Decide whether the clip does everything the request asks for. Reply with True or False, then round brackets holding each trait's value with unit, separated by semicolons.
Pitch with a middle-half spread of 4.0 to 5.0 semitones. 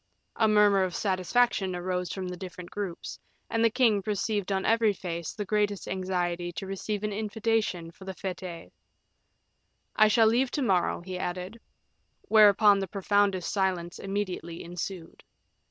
False (2.7 semitones)